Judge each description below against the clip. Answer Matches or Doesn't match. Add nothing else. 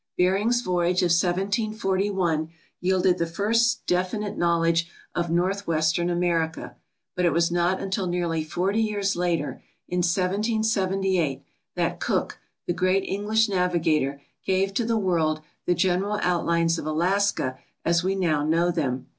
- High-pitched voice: Doesn't match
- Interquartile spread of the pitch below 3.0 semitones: Matches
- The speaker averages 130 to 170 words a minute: Matches